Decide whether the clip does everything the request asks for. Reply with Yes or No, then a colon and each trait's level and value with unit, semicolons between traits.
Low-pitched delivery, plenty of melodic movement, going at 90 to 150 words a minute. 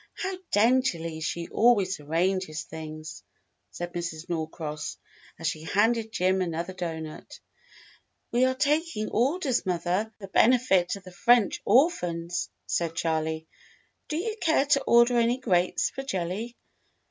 No: medium, 185 Hz; wide, 6.4 semitones; slow, 135 wpm